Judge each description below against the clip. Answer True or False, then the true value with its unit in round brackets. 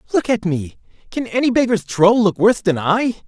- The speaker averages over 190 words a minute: True (200 wpm)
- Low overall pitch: False (205 Hz)